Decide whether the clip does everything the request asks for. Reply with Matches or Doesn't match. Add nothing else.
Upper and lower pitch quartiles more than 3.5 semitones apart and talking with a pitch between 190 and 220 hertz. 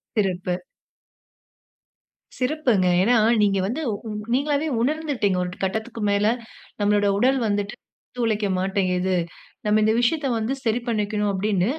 Matches